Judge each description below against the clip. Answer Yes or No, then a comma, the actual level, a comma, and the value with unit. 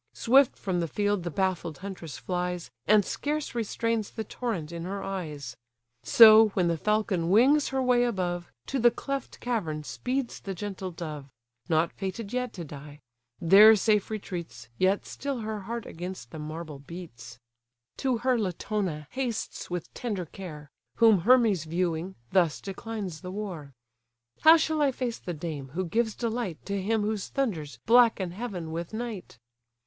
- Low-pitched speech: No, high, 195 Hz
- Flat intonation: No, average, 5.3 semitones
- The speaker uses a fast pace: No, average, 160 wpm